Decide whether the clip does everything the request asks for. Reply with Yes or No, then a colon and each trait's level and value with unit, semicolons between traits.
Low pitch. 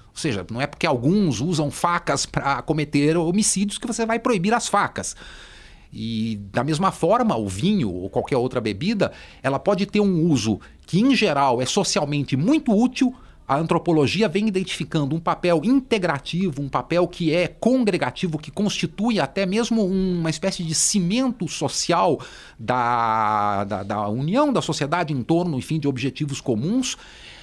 No: medium, 170 Hz